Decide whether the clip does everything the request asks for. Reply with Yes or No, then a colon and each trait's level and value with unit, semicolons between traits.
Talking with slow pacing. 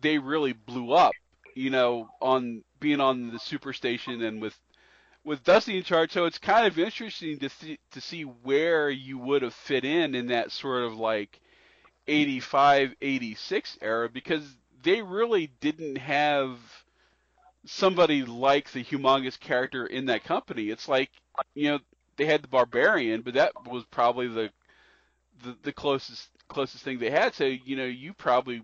No: average, 170 wpm